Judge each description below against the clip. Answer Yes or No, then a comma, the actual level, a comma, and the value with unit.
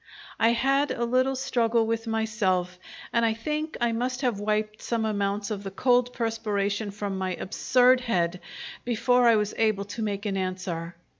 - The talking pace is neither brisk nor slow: Yes, average, 170 wpm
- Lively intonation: No, average, 3.3 semitones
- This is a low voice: No, high, 220 Hz